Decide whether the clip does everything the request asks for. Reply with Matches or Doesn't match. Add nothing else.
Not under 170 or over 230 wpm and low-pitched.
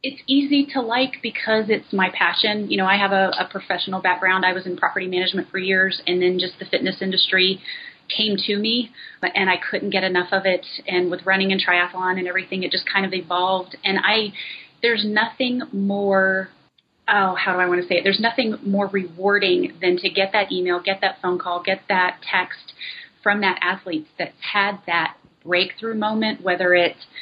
Doesn't match